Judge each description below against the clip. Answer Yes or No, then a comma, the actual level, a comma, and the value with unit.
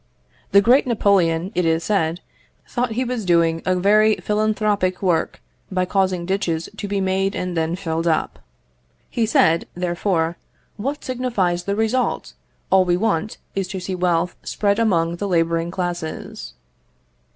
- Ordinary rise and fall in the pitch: Yes, average, 3.6 semitones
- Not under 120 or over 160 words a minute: Yes, average, 150 wpm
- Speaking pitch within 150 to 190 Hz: Yes, medium, 185 Hz